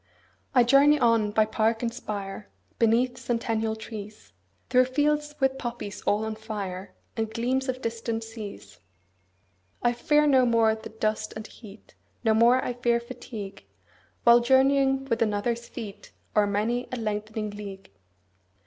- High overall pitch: Yes, high, 230 Hz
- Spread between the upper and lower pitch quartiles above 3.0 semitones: No, average, 2.7 semitones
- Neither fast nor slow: Yes, average, 150 wpm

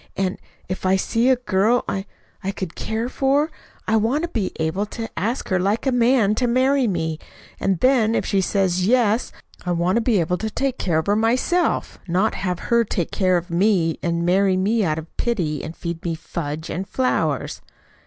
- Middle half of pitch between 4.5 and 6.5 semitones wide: Yes, average, 4.9 semitones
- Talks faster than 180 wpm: Yes, fast, 205 wpm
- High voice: Yes, high, 195 Hz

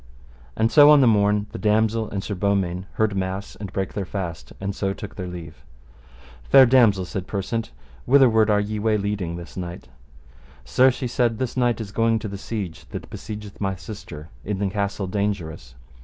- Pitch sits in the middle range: No, low, 100 Hz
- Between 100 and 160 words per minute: No, average, 185 wpm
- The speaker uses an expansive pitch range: No, average, 2.8 semitones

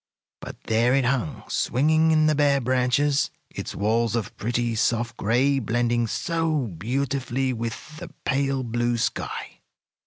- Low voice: Yes, low, 125 Hz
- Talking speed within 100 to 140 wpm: Yes, slow, 135 wpm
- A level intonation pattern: No, average, 3.1 semitones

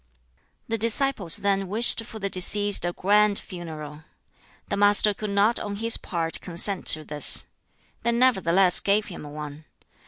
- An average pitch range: Yes, average, 3.8 semitones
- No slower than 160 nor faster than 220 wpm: No, average, 150 wpm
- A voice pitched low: No, high, 200 Hz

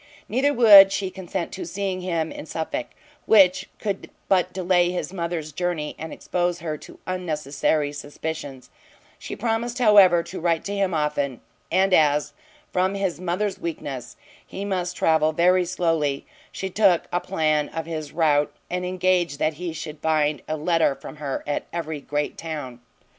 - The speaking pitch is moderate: Yes, medium, 170 Hz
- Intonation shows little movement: No, average, 3.4 semitones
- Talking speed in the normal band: Yes, average, 160 wpm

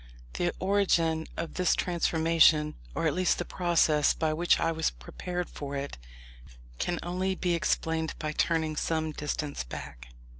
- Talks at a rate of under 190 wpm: Yes, average, 150 wpm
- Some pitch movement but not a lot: No, narrow, 2.3 semitones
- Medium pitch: Yes, medium, 165 Hz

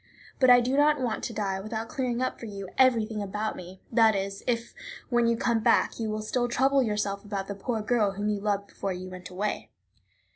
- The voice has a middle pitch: No, high, 215 Hz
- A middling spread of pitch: Yes, average, 3.3 semitones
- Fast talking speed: Yes, fast, 220 wpm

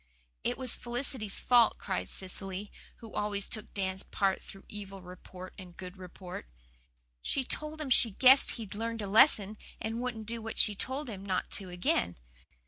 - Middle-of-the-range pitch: No, high, 210 Hz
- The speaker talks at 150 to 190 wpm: Yes, average, 170 wpm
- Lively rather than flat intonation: No, average, 3.6 semitones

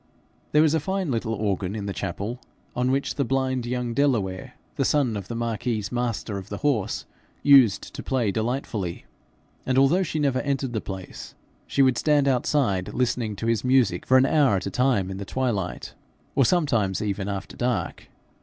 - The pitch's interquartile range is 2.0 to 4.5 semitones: No, average, 4.9 semitones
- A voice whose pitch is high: No, low, 120 Hz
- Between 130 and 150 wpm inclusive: No, average, 180 wpm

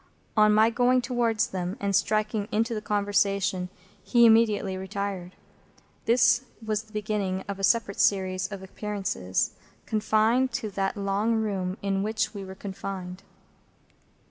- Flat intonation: Yes, narrow, 2.3 semitones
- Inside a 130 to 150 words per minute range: Yes, average, 140 wpm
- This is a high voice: Yes, high, 205 Hz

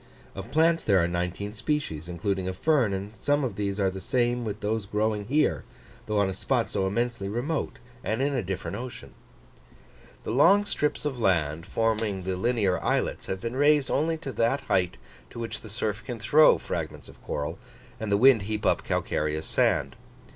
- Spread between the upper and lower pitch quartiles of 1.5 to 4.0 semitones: No, average, 5.2 semitones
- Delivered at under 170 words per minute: No, average, 190 wpm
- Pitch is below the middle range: Yes, low, 110 Hz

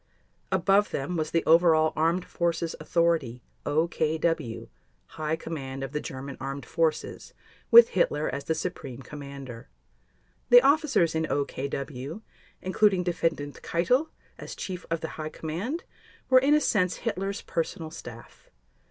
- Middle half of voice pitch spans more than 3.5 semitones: Yes, average, 4.0 semitones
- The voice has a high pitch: No, medium, 160 Hz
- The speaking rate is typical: No, slow, 130 wpm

